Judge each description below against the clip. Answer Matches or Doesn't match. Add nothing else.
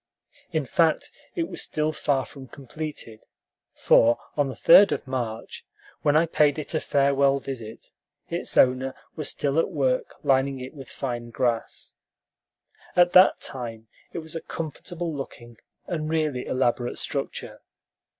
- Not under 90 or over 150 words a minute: Matches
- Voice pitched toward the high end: Doesn't match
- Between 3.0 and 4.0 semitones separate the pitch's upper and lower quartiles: Matches